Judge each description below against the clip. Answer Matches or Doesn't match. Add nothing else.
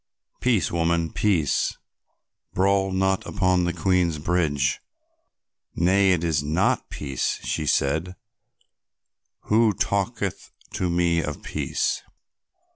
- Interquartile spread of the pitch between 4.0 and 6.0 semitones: Doesn't match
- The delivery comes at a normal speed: Doesn't match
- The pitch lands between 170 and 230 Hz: Doesn't match